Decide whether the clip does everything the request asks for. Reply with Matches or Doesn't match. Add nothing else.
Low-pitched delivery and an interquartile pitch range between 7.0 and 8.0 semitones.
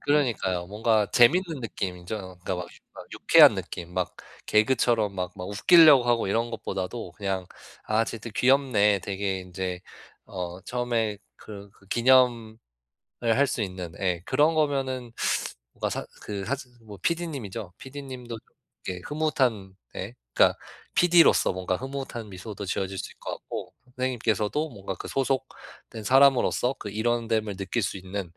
Doesn't match